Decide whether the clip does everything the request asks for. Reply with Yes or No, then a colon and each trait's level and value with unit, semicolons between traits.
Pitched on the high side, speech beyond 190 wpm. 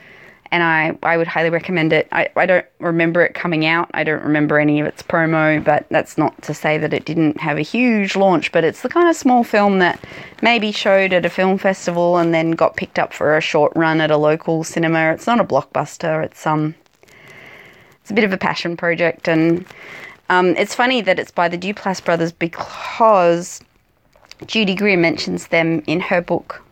No: medium, 170 Hz; fast, 205 wpm